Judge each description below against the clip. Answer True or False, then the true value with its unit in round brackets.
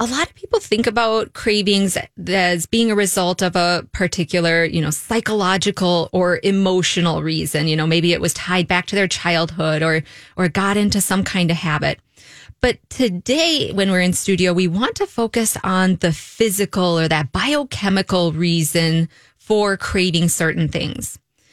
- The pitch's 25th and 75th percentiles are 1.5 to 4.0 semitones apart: True (3.3 semitones)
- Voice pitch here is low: False (180 Hz)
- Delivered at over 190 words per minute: False (165 wpm)